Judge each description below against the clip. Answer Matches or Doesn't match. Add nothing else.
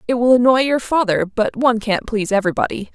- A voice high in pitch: Matches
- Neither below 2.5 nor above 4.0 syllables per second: Doesn't match